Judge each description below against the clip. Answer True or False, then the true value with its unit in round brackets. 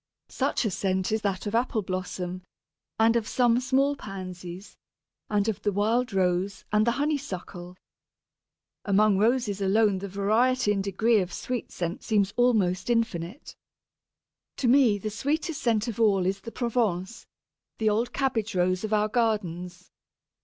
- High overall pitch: True (210 Hz)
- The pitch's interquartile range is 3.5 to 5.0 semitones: True (3.8 semitones)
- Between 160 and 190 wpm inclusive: False (145 wpm)